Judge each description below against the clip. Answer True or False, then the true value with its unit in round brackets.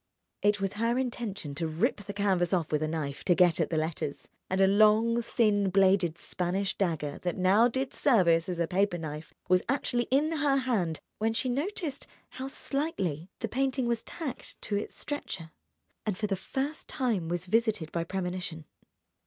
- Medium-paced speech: True (180 wpm)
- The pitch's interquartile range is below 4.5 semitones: False (5.6 semitones)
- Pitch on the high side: True (195 Hz)